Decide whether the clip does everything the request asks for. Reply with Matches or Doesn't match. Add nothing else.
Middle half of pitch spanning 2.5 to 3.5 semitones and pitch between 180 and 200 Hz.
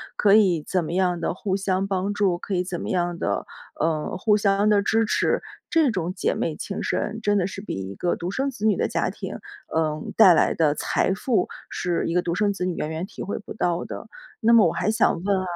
Matches